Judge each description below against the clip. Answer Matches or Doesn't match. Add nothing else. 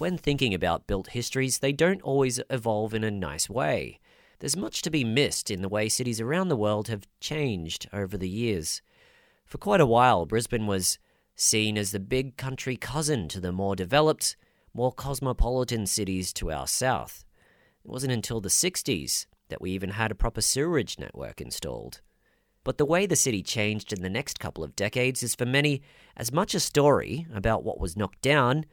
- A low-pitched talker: Matches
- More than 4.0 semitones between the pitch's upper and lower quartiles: Matches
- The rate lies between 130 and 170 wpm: Doesn't match